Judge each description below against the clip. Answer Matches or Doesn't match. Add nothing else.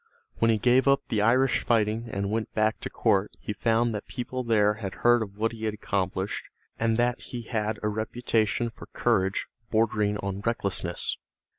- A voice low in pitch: Matches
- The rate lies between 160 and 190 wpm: Matches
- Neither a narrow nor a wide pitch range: Doesn't match